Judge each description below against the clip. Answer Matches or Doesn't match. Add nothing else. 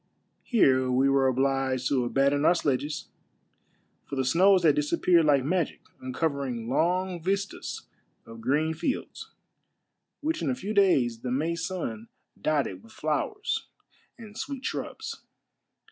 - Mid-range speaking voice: Matches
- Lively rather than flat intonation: Matches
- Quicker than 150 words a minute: Doesn't match